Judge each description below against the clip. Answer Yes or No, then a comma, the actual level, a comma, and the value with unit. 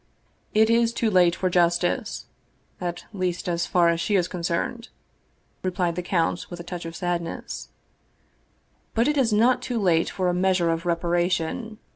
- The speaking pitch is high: No, medium, 180 Hz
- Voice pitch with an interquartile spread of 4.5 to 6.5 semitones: No, average, 3.6 semitones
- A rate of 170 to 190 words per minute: Yes, average, 180 wpm